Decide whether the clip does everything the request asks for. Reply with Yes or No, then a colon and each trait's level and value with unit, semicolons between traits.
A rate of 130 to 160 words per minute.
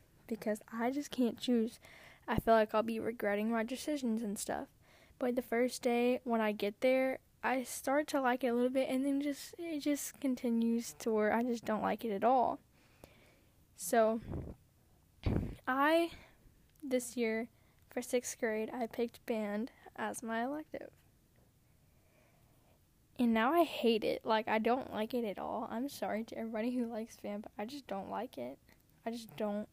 No: average, 175 wpm